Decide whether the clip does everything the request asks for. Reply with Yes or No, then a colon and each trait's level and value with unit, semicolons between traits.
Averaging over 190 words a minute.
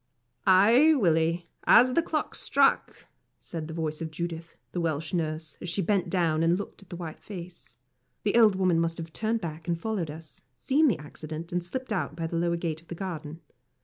Yes: fast, 205 wpm